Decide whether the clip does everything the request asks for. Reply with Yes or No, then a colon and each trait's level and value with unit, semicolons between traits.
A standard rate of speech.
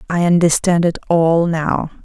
Yes: average, 145 wpm